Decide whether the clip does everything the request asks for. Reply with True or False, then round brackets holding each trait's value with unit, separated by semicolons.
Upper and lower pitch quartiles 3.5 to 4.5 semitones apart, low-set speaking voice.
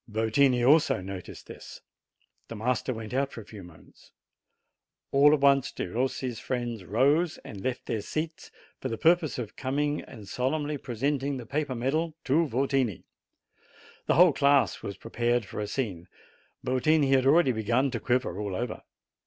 True (4.0 semitones; 130 Hz)